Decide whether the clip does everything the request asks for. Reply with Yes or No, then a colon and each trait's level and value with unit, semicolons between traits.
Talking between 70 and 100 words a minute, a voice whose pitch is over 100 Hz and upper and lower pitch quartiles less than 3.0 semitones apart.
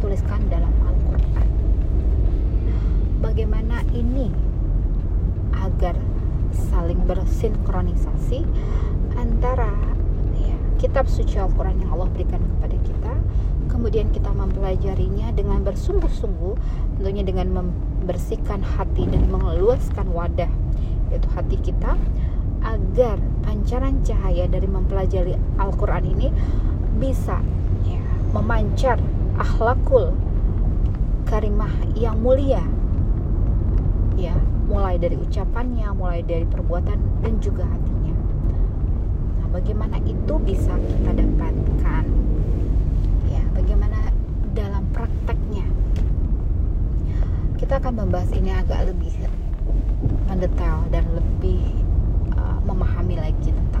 No: average, 90 wpm; very low, 90 Hz; narrow, 2.5 semitones